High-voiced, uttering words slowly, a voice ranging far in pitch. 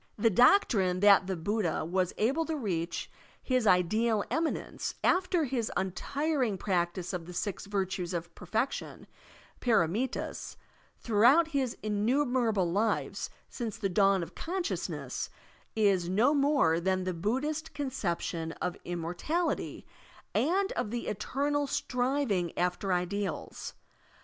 Yes: high, 210 Hz; slow, 120 wpm; wide, 6.9 semitones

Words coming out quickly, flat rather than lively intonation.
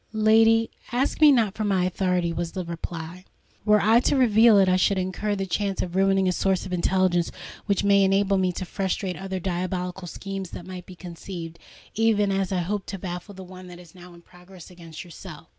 Yes: fast, 210 wpm; narrow, 2.1 semitones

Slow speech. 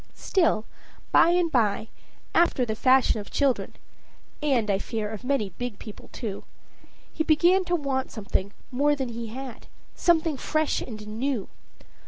No: average, 150 wpm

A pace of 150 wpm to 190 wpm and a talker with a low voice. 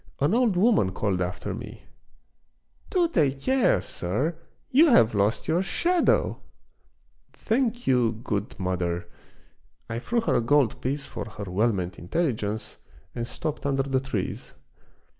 Yes: average, 160 wpm; low, 130 Hz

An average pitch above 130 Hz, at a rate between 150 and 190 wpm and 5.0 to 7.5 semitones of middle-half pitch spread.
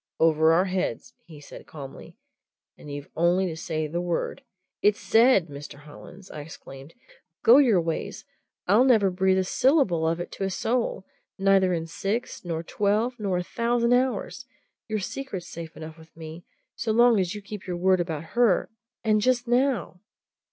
Yes: medium, 185 Hz; average, 175 wpm; wide, 5.5 semitones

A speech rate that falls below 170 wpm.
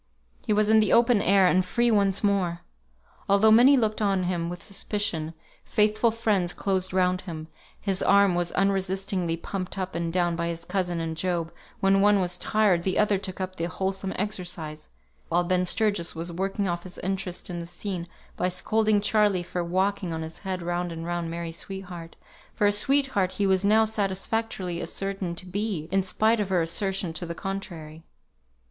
No: average, 185 wpm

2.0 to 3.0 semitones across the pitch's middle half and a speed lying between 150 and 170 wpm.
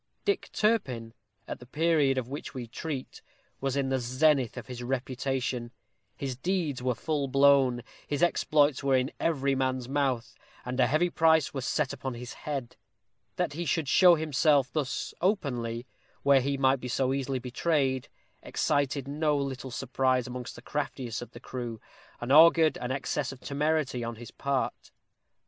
Yes: average, 2.7 semitones; average, 165 wpm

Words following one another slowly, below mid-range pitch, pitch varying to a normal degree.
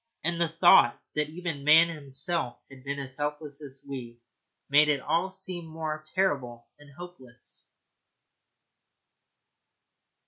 No: slow, 125 wpm; medium, 150 Hz; average, 3.6 semitones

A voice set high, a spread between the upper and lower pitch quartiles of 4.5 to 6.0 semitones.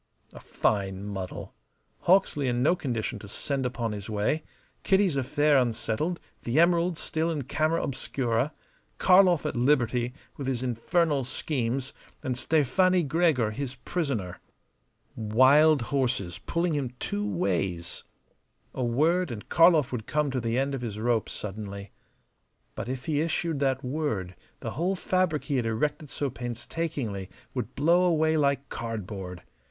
No: low, 130 Hz; wide, 5.5 semitones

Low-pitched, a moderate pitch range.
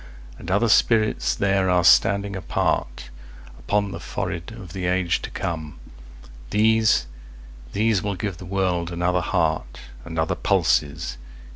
No: very low, 90 Hz; wide, 7.8 semitones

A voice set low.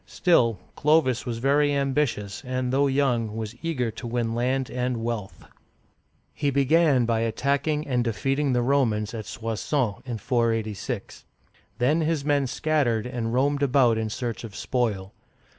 Yes: low, 125 Hz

